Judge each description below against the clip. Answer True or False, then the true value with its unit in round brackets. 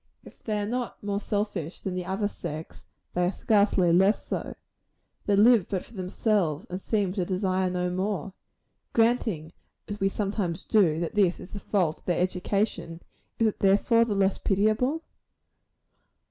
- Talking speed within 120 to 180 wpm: True (165 wpm)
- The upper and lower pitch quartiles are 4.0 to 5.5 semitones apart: False (2.8 semitones)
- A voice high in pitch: True (195 Hz)